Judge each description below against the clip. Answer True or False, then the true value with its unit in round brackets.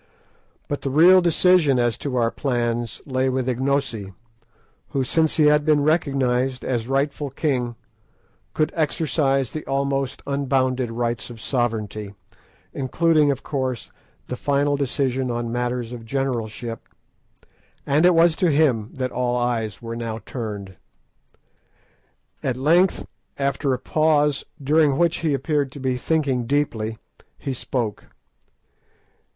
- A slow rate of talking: True (130 wpm)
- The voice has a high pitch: False (135 Hz)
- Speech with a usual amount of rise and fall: True (3.3 semitones)